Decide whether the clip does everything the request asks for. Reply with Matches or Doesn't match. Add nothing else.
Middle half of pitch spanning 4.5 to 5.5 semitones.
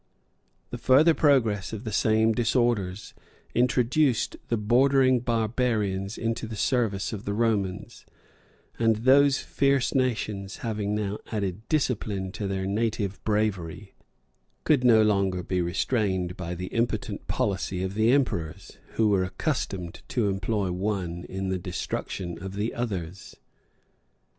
Doesn't match